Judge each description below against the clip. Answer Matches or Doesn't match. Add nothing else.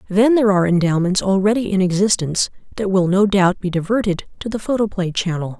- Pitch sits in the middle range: Doesn't match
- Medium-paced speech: Matches